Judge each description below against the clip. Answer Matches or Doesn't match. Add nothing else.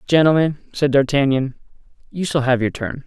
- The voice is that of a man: Matches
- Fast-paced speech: Doesn't match